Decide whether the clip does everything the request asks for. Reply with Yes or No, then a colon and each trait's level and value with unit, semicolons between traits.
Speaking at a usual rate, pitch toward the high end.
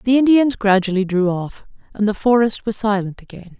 Yes: average, 185 wpm; high, 210 Hz